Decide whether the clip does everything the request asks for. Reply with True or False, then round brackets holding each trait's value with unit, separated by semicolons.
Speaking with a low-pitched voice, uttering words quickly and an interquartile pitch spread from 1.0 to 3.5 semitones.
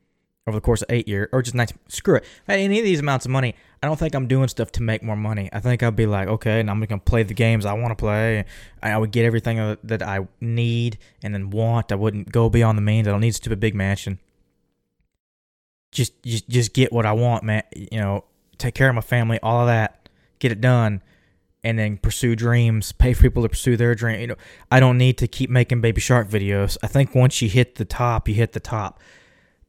True (115 Hz; 245 wpm; 2.4 semitones)